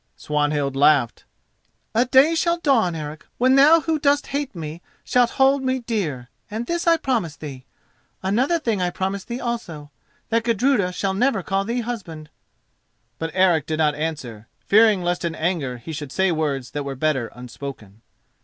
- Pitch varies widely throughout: Yes, wide, 8.5 semitones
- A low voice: No, medium, 185 Hz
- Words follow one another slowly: No, average, 175 wpm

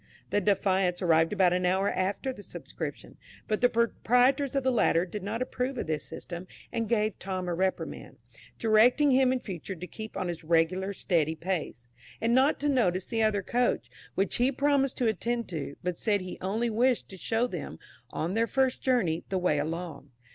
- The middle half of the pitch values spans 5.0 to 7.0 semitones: Yes, average, 5.3 semitones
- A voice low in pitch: No, high, 205 Hz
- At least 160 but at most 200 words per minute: Yes, average, 195 wpm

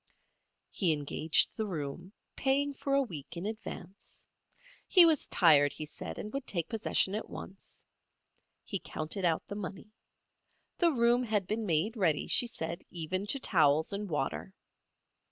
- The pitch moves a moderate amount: No, wide, 5.8 semitones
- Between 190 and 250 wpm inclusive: No, average, 155 wpm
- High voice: Yes, high, 195 Hz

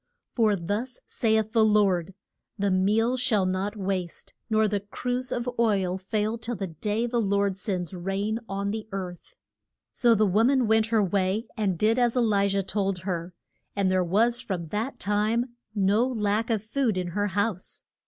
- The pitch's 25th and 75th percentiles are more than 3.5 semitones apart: No, average, 2.8 semitones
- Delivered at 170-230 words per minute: Yes, average, 180 wpm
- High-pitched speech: Yes, high, 205 Hz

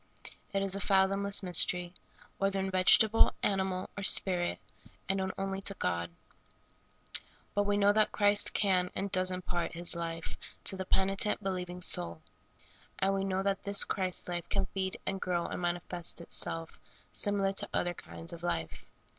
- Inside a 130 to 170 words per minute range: Yes, average, 165 wpm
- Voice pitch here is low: No, high, 190 Hz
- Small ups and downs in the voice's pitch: Yes, narrow, 1.9 semitones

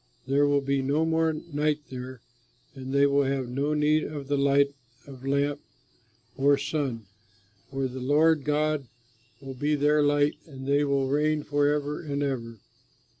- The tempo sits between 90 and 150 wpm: No, average, 160 wpm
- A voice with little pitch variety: Yes, narrow, 1.6 semitones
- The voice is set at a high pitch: No, medium, 140 Hz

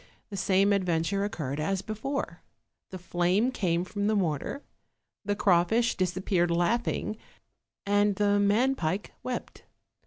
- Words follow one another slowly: Yes, slow, 125 wpm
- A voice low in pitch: No, high, 200 Hz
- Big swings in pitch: No, average, 3.1 semitones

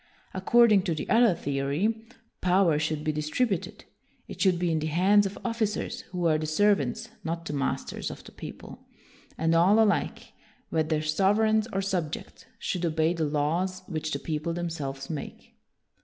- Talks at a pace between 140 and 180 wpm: Yes, average, 170 wpm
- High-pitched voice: No, medium, 170 Hz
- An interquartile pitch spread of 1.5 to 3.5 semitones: No, average, 4.2 semitones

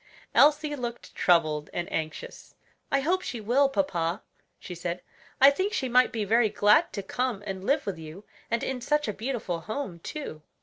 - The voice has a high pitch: Yes, high, 230 Hz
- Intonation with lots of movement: Yes, wide, 7.6 semitones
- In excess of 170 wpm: Yes, average, 180 wpm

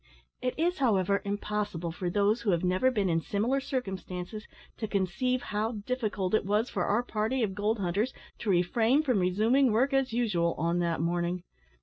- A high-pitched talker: Yes, high, 210 Hz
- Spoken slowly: No, average, 180 wpm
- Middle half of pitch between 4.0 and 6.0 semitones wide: Yes, average, 4.8 semitones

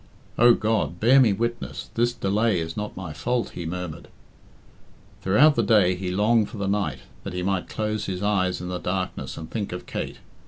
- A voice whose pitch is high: No, low, 100 Hz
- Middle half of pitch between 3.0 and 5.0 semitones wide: Yes, average, 3.7 semitones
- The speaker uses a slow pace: No, average, 195 wpm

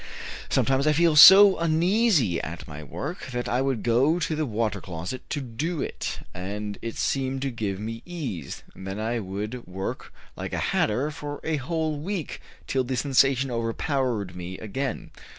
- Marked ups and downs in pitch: Yes, wide, 6.2 semitones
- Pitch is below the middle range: Yes, low, 130 Hz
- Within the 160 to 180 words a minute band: Yes, average, 170 wpm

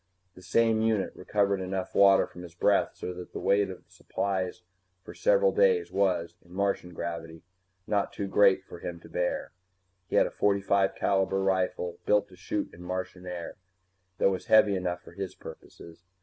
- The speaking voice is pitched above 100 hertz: No, very low, 95 Hz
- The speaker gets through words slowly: No, average, 175 wpm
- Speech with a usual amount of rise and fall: No, narrow, 2.1 semitones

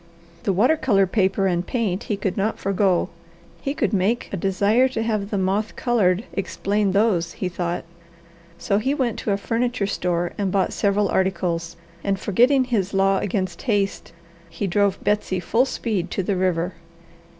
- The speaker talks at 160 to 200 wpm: Yes, average, 170 wpm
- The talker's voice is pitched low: No, high, 200 Hz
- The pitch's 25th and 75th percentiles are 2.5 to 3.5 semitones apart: Yes, average, 2.8 semitones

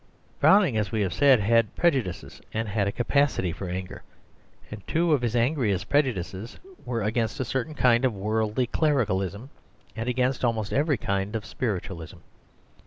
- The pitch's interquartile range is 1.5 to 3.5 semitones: No, average, 4.5 semitones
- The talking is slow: No, average, 160 wpm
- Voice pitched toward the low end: Yes, low, 115 Hz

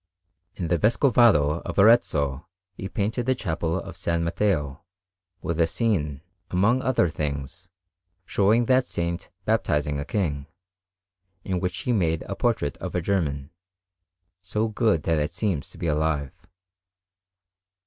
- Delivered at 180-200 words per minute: No, average, 140 wpm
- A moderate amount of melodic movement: No, wide, 5.8 semitones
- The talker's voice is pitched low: Yes, very low, 85 Hz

